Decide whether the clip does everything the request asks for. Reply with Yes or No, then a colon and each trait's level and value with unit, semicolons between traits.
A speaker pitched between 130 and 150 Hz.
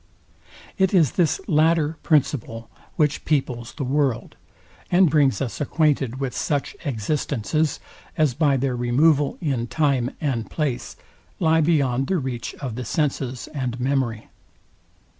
Yes: medium, 140 Hz